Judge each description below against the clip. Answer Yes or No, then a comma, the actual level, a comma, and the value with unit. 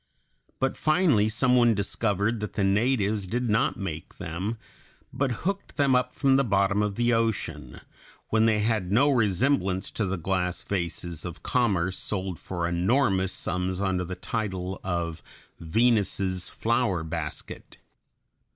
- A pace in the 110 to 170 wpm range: Yes, average, 140 wpm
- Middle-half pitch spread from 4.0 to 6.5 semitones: Yes, average, 4.5 semitones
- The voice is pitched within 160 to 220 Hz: No, low, 100 Hz